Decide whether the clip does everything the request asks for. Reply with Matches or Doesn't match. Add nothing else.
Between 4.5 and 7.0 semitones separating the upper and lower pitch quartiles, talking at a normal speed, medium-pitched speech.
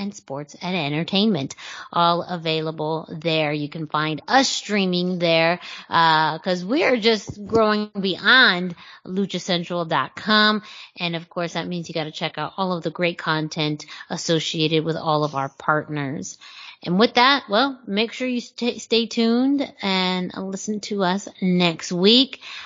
Matches